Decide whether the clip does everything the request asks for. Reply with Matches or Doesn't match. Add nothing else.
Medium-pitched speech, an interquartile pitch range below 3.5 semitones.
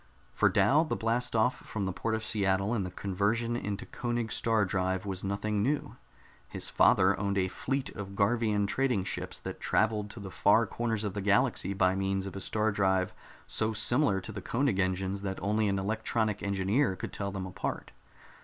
Doesn't match